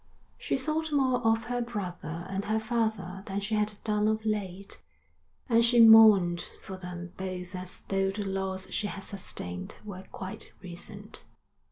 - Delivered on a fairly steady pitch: No, average, 3.0 semitones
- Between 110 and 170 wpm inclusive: Yes, average, 160 wpm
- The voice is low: No, high, 200 Hz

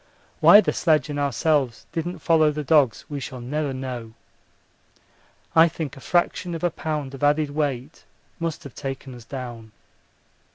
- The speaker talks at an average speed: Yes, average, 160 wpm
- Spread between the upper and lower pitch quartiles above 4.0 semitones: No, average, 3.4 semitones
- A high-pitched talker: No, medium, 145 Hz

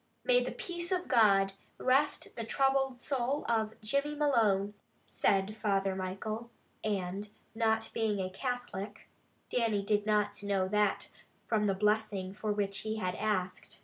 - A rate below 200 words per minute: Yes, average, 140 wpm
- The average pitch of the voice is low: No, high, 215 Hz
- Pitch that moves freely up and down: No, average, 3.5 semitones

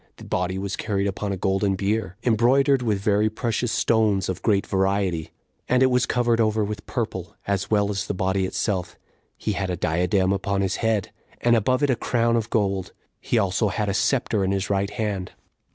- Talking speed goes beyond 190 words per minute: Yes, average, 200 wpm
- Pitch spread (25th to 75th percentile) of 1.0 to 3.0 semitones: Yes, narrow, 2.6 semitones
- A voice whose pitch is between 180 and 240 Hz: No, low, 100 Hz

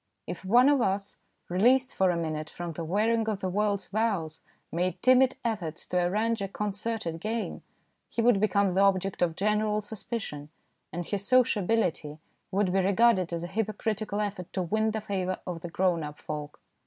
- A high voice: Yes, high, 195 Hz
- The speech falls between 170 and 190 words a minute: Yes, average, 180 wpm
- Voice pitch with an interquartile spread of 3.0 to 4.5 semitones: Yes, average, 3.7 semitones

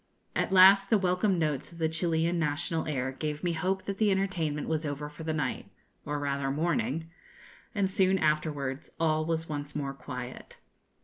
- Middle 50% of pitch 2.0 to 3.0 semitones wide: No, average, 3.6 semitones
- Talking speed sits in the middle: Yes, average, 175 wpm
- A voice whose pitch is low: No, medium, 160 Hz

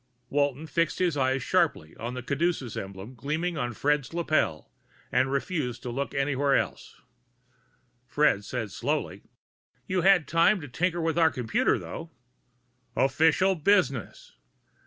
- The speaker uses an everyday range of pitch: Yes, average, 4.7 semitones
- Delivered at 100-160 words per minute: Yes, slow, 135 wpm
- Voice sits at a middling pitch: Yes, medium, 145 Hz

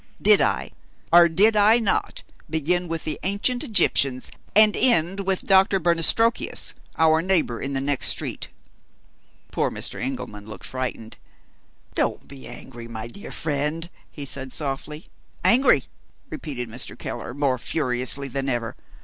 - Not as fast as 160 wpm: Yes, average, 140 wpm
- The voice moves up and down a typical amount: No, wide, 6.3 semitones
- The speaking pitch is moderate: Yes, medium, 150 Hz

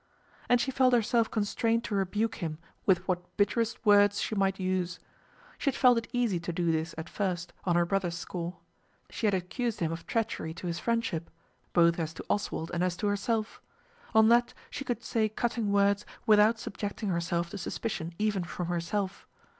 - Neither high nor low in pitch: No, high, 200 Hz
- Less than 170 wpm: No, average, 185 wpm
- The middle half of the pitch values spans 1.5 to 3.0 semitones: No, average, 4.5 semitones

